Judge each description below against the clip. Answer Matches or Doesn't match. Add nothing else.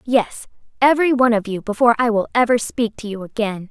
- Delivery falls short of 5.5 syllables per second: Doesn't match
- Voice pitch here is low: Doesn't match